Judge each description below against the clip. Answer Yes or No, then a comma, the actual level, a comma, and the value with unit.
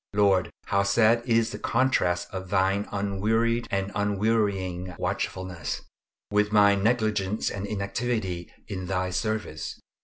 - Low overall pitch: Yes, low, 100 Hz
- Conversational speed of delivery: No, slow, 120 wpm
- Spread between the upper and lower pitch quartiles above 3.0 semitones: No, narrow, 2.6 semitones